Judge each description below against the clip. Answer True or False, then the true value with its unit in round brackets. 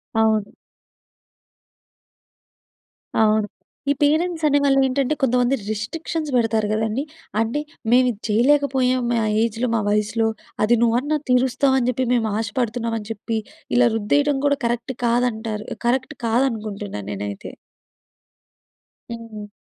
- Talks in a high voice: True (235 Hz)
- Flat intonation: False (3.3 semitones)